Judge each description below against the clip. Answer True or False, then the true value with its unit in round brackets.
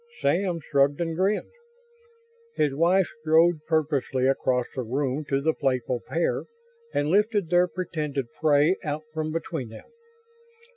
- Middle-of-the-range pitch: True (155 Hz)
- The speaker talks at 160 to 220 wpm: False (135 wpm)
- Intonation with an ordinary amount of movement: True (3.6 semitones)